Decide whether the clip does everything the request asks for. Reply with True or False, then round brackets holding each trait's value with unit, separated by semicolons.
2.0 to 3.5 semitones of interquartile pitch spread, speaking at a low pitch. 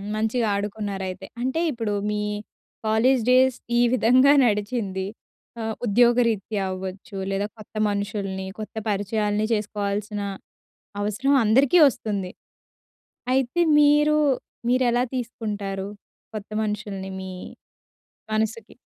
False (3.2 semitones; 215 Hz)